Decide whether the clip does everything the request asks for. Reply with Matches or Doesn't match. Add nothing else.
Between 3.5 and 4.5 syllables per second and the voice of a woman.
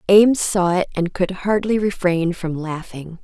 Matches